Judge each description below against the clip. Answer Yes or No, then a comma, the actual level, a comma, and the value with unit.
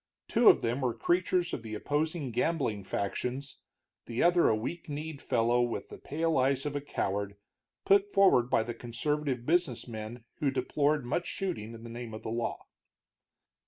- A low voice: Yes, low, 130 Hz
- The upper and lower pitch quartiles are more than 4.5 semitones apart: Yes, average, 5.0 semitones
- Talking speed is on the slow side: No, average, 175 wpm